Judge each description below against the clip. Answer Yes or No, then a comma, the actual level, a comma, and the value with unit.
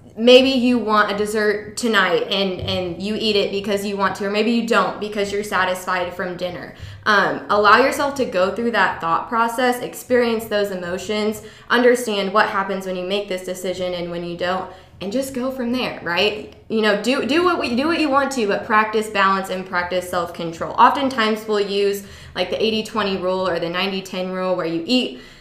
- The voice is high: Yes, high, 205 Hz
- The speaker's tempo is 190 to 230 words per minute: Yes, average, 200 wpm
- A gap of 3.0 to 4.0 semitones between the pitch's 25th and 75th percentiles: Yes, average, 3.7 semitones